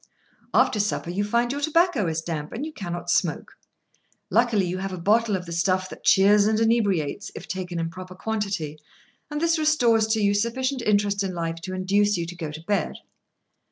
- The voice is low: No, high, 200 Hz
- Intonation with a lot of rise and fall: No, average, 4.3 semitones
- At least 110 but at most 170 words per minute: No, average, 195 wpm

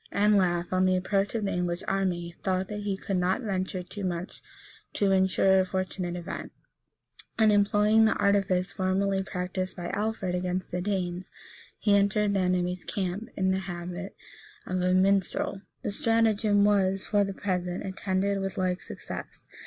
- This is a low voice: No, high, 190 Hz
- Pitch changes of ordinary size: No, narrow, 1.8 semitones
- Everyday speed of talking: Yes, average, 160 wpm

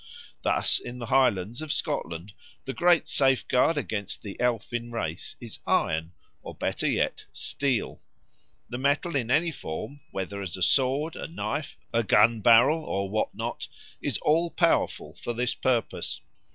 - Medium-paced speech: Yes, average, 150 wpm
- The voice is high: No, low, 120 Hz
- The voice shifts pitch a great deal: Yes, wide, 5.8 semitones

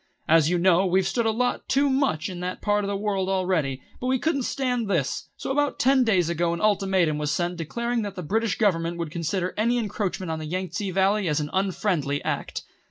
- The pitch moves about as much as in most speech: Yes, average, 4.5 semitones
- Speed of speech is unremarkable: No, fast, 225 wpm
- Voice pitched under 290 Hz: Yes, high, 190 Hz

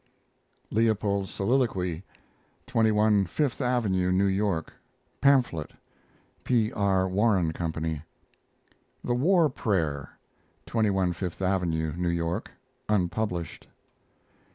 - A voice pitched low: Yes, very low, 95 Hz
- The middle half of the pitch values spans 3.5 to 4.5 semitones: Yes, average, 4.2 semitones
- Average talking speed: No, slow, 85 wpm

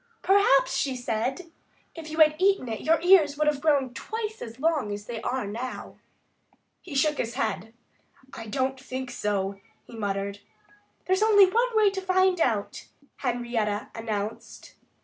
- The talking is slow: No, average, 155 wpm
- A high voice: Yes, very high, 265 Hz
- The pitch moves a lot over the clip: Yes, wide, 7.9 semitones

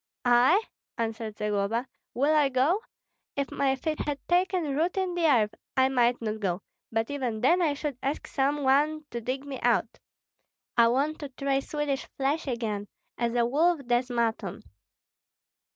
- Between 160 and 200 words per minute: Yes, average, 165 wpm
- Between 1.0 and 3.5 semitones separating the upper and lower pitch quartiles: No, average, 4.1 semitones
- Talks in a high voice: Yes, very high, 270 Hz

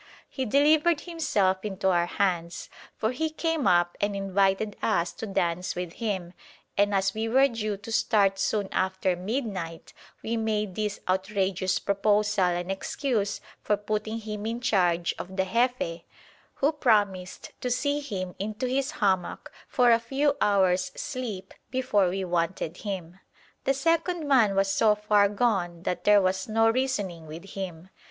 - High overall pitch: Yes, high, 205 Hz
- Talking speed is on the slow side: No, average, 155 wpm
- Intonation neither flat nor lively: Yes, average, 3.9 semitones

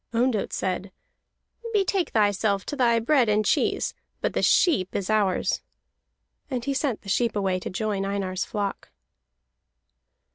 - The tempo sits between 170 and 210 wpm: No, average, 140 wpm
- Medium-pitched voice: No, high, 215 Hz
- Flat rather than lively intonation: No, average, 3.8 semitones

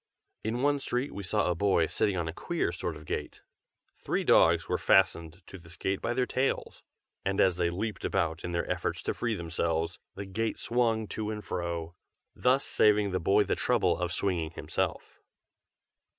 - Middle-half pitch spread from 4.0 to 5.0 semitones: Yes, average, 4.5 semitones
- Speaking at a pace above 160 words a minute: Yes, average, 185 wpm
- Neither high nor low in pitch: No, very low, 95 Hz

